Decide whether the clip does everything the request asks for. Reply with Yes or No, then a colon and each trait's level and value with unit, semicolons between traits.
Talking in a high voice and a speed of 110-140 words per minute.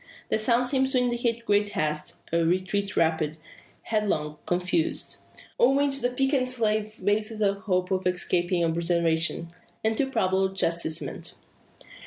Yes: high, 200 Hz; slow, 135 wpm